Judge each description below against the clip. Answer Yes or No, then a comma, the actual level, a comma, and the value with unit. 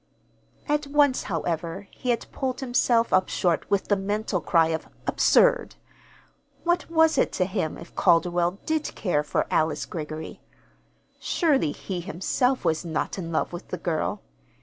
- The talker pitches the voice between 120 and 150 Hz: No, high, 190 Hz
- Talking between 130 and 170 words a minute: Yes, average, 150 wpm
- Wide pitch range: Yes, wide, 7.6 semitones